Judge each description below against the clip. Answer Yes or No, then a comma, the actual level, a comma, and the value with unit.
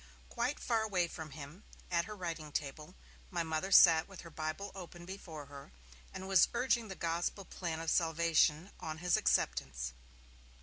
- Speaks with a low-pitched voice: No, medium, 170 Hz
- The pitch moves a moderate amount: Yes, average, 3.5 semitones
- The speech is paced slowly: No, average, 165 wpm